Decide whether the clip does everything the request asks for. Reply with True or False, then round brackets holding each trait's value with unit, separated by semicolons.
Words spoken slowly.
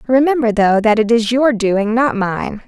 False (200 wpm)